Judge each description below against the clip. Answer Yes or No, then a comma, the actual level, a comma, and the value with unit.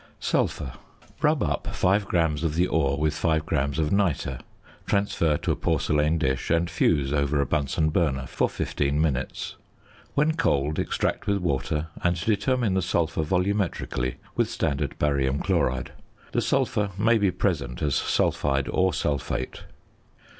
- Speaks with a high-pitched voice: No, very low, 80 Hz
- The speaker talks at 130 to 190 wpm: Yes, average, 145 wpm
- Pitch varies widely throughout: No, average, 4.4 semitones